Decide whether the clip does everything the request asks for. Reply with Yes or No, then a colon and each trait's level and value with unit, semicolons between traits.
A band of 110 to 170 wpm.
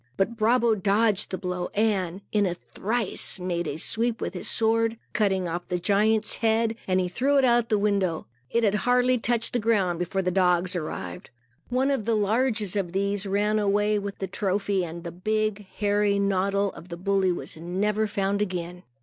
No: average, 185 wpm